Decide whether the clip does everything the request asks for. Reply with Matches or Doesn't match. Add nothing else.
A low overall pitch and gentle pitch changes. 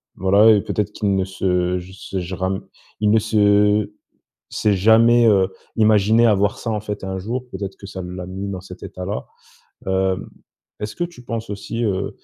Matches